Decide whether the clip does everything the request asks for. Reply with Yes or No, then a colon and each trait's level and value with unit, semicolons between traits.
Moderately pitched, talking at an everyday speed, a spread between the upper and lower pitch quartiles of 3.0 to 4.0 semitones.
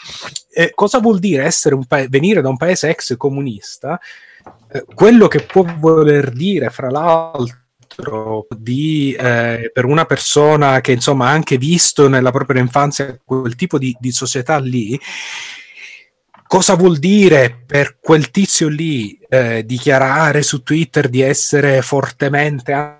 Yes: medium, 145 Hz; average, 140 wpm; average, 3.6 semitones